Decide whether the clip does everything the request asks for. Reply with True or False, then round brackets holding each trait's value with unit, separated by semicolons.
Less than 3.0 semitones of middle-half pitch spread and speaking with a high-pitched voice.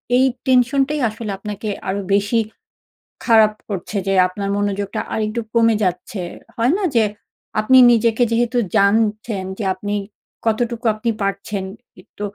True (2.5 semitones; 215 Hz)